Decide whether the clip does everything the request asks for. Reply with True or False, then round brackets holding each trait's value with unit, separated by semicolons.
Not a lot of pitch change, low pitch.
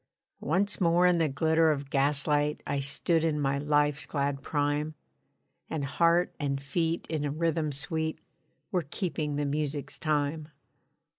False (2.3 semitones; 150 Hz)